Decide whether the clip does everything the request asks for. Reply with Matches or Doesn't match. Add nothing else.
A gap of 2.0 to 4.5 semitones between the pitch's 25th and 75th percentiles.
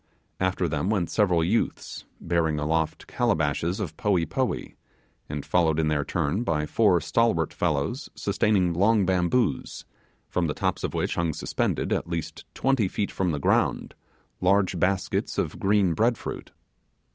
Matches